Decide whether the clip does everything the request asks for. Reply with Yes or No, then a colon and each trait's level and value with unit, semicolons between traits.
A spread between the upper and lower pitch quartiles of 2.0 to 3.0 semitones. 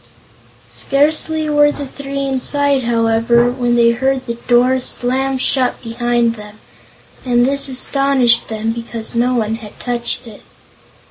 Yes: narrow, 2.6 semitones